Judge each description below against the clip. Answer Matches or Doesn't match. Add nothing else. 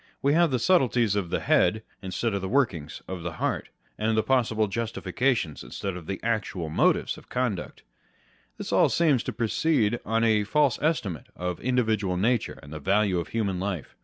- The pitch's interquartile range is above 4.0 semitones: Matches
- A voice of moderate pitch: Doesn't match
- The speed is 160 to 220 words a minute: Matches